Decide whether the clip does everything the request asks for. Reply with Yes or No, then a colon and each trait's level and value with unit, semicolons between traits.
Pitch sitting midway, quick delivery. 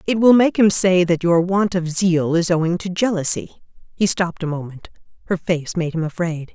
Yes: medium, 180 Hz; fast, 210 wpm